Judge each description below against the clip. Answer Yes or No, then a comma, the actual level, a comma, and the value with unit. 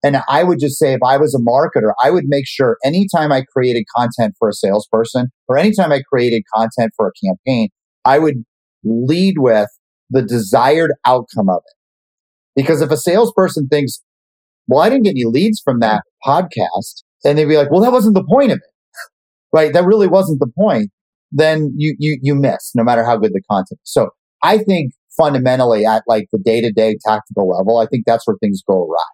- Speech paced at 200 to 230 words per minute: Yes, fast, 205 wpm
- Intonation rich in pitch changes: Yes, wide, 5.9 semitones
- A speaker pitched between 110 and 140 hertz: Yes, low, 135 Hz